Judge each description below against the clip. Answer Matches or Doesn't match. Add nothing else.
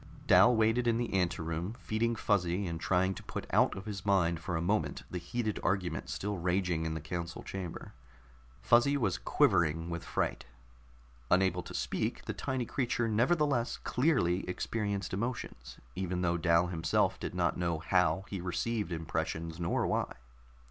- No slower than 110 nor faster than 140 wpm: Doesn't match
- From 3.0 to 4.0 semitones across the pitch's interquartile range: Doesn't match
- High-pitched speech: Doesn't match